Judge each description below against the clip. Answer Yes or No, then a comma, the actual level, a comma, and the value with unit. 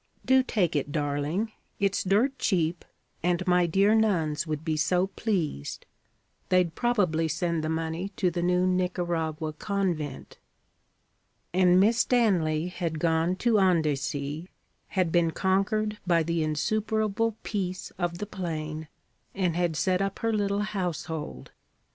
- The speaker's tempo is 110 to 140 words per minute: Yes, slow, 135 wpm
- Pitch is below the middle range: No, medium, 180 Hz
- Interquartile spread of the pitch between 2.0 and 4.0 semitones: Yes, average, 3.6 semitones